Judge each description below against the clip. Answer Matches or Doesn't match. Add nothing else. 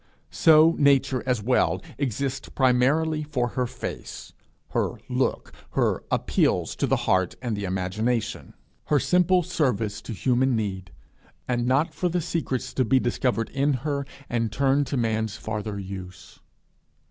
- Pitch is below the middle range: Matches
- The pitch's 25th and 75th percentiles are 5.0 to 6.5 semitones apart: Doesn't match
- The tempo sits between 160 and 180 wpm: Doesn't match